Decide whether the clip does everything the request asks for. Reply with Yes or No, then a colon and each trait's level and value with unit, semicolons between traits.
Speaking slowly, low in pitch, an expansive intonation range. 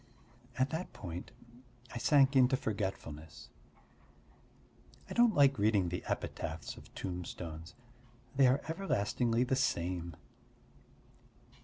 Yes: slow, 105 wpm; low, 110 Hz; wide, 7.5 semitones